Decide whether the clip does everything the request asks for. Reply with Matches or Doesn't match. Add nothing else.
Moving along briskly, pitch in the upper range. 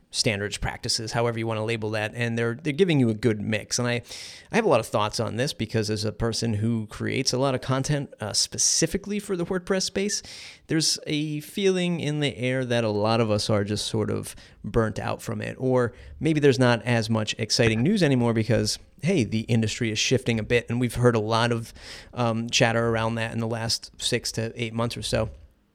Doesn't match